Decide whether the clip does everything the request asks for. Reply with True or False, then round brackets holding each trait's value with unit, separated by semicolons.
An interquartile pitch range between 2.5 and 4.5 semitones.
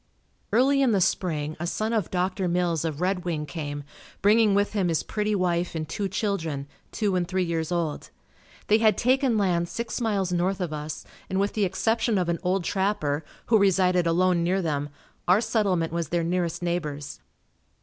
True (3.3 semitones)